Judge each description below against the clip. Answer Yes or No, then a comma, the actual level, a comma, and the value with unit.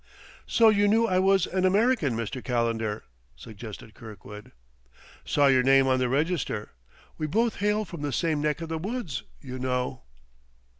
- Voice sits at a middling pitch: Yes, medium, 145 Hz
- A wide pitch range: Yes, wide, 7.6 semitones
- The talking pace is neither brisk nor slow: Yes, average, 160 wpm